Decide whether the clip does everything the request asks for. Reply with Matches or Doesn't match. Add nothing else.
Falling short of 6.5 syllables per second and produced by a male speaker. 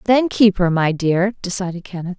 Doesn't match